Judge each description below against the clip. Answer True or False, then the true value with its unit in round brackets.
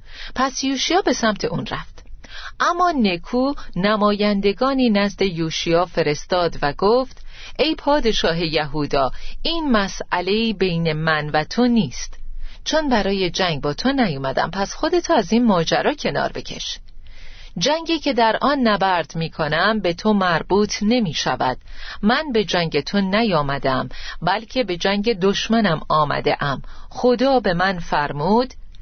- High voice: True (205 Hz)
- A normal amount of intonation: False (6.1 semitones)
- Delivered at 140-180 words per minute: False (130 wpm)